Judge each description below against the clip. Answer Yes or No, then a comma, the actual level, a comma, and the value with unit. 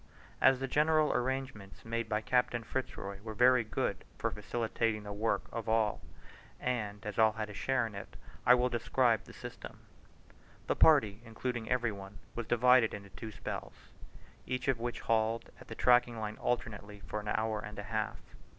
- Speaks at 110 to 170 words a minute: No, average, 180 wpm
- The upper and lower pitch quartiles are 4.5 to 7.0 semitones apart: No, average, 2.8 semitones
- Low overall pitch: Yes, low, 115 Hz